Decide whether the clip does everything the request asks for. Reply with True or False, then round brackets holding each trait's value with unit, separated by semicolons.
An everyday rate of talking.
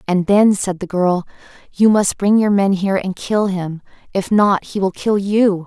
False (210 wpm)